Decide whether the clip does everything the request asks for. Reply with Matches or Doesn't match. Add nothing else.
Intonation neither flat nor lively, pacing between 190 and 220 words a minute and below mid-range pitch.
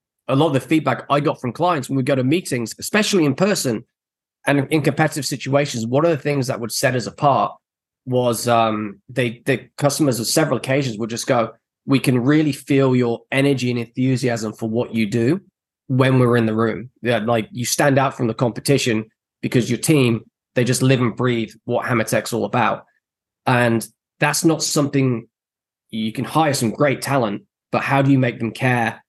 Matches